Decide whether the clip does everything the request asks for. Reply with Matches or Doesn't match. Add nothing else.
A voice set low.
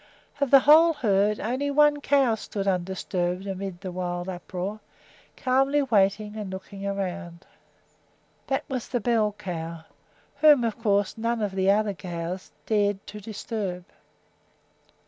Doesn't match